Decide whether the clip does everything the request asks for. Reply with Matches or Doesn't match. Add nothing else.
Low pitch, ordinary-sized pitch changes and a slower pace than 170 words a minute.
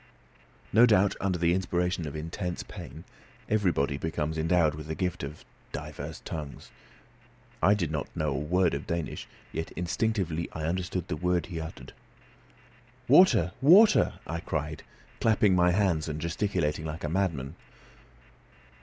Matches